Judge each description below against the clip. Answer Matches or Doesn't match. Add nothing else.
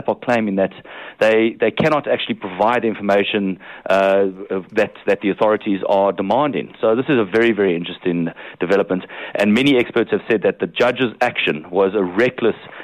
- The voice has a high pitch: Doesn't match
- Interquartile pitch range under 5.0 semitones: Matches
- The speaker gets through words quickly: Doesn't match